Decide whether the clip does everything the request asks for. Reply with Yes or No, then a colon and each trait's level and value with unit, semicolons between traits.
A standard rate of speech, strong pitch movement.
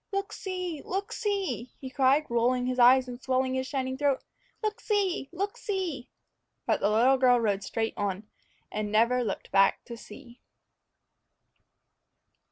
Yes: average, 150 wpm; wide, 6.3 semitones